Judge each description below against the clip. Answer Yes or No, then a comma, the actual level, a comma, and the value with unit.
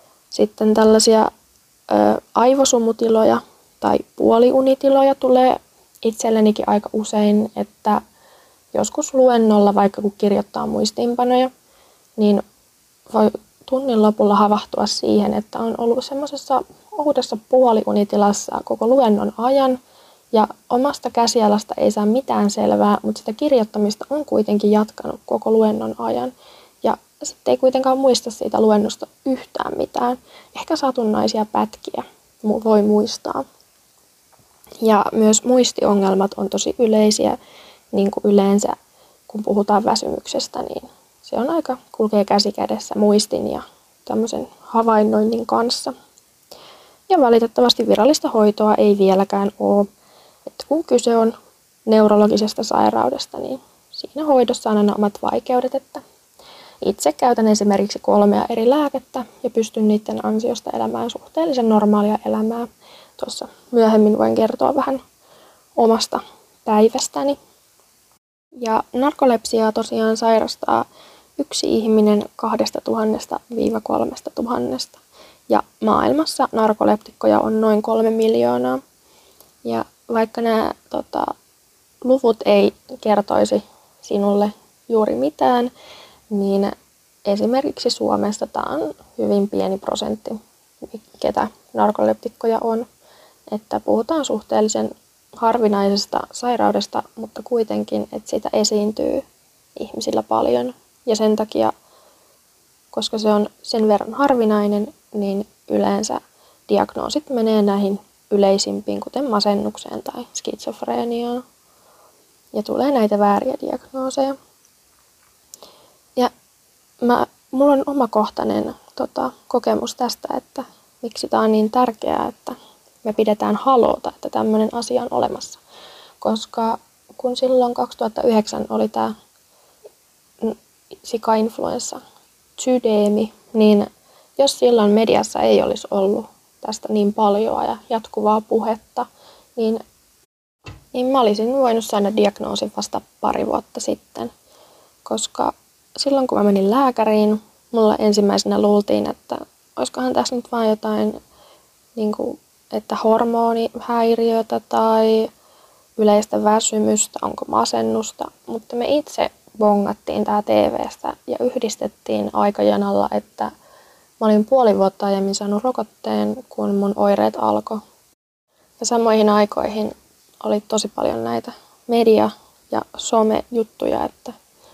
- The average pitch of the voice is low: No, high, 220 Hz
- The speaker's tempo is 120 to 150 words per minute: No, average, 105 wpm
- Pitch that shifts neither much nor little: Yes, average, 3.2 semitones